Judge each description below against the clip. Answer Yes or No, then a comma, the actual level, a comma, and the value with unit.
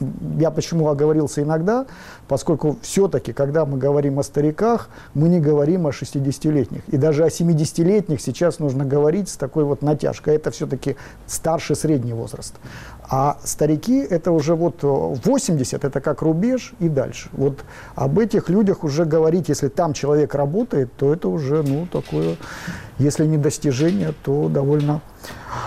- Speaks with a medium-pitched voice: Yes, medium, 150 Hz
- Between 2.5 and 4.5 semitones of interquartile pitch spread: Yes, average, 2.9 semitones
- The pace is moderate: Yes, average, 145 wpm